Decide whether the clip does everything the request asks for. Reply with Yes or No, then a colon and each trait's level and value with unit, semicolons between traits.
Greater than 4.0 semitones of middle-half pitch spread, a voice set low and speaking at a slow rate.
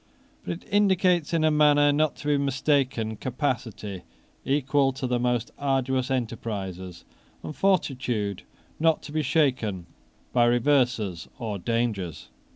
Yes: average, 4.7 semitones; low, 130 Hz; slow, 130 wpm